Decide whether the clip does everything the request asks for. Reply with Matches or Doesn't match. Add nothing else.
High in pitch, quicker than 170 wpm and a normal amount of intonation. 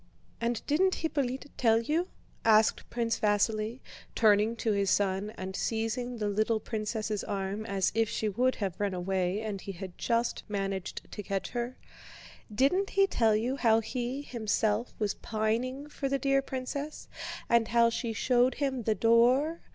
Doesn't match